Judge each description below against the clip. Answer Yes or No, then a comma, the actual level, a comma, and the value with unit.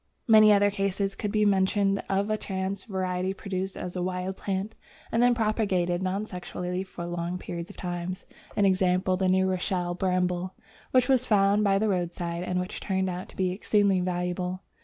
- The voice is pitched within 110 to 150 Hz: No, high, 190 Hz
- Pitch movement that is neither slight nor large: No, narrow, 1.8 semitones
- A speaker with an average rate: Yes, average, 175 wpm